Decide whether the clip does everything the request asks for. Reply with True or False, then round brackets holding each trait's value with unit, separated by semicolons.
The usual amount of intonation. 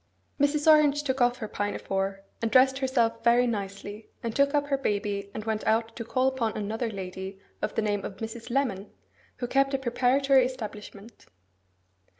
True (4.3 semitones)